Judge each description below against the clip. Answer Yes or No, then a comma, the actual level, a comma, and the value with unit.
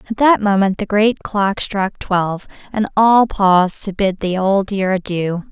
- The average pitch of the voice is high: Yes, high, 200 Hz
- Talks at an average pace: Yes, average, 185 wpm